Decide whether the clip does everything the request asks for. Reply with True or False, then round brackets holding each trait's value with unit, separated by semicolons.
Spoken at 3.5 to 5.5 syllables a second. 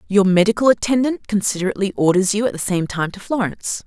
False (6.6 syllables/s)